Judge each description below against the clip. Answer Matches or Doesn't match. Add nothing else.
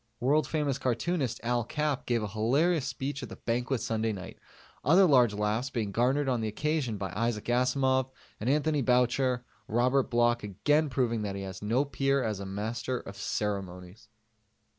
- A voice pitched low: Matches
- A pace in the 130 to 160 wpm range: Doesn't match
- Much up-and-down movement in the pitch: Doesn't match